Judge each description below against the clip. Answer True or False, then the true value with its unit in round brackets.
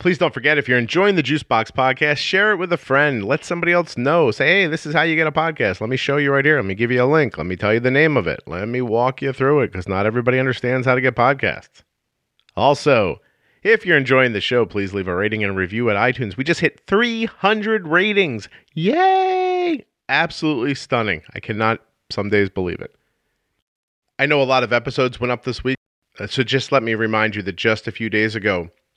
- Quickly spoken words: True (235 wpm)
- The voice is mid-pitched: False (130 Hz)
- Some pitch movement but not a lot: False (6.0 semitones)